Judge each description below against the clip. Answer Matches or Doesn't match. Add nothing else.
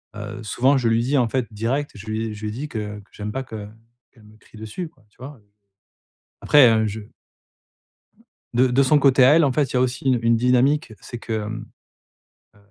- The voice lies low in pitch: Matches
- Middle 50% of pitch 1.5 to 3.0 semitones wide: Doesn't match